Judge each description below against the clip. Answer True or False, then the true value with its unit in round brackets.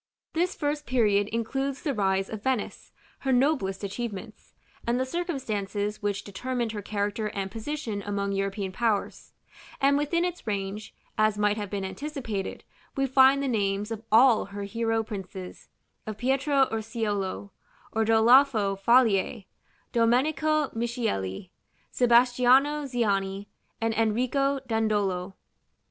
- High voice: True (225 Hz)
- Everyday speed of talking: False (125 wpm)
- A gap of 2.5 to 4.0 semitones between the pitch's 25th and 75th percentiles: False (4.5 semitones)